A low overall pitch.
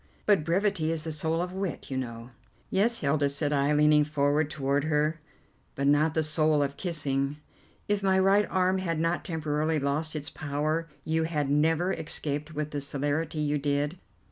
No: medium, 155 Hz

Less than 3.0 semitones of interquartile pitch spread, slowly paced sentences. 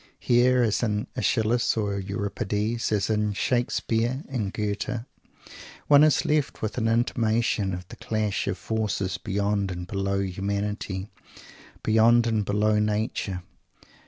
Yes: narrow, 2.5 semitones; slow, 130 wpm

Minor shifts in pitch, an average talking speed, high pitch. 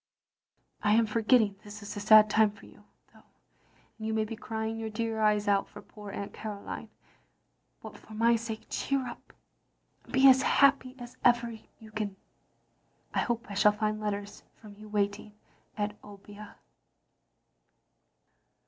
Yes: narrow, 1.7 semitones; average, 155 wpm; high, 215 Hz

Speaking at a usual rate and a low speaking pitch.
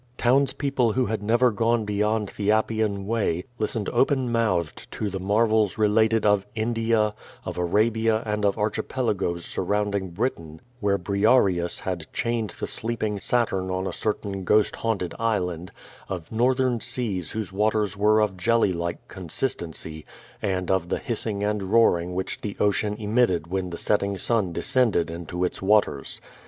Yes: average, 150 wpm; low, 105 Hz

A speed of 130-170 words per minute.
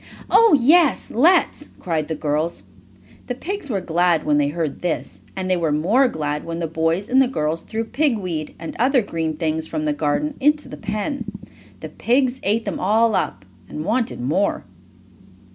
No: average, 180 wpm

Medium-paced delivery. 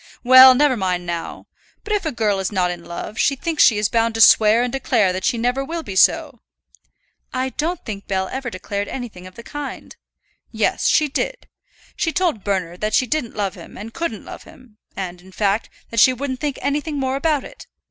No: fast, 210 wpm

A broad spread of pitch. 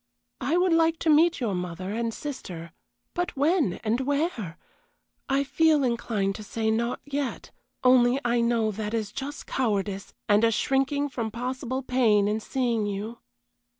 No: average, 4.6 semitones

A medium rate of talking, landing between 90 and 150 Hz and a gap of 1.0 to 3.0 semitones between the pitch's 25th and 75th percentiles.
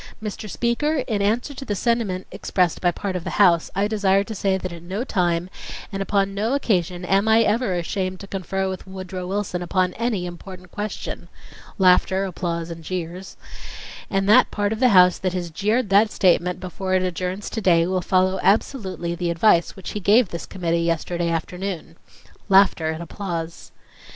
No: average, 180 wpm; high, 190 Hz; narrow, 2.6 semitones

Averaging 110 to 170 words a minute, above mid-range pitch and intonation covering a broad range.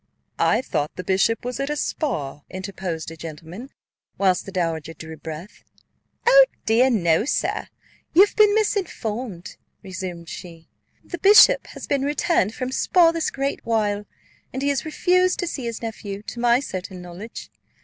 Yes: average, 160 wpm; high, 220 Hz; wide, 7.9 semitones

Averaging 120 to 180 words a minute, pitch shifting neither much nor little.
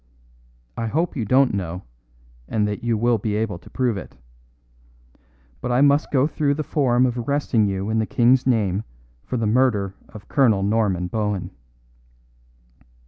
Yes: average, 160 wpm; average, 3.9 semitones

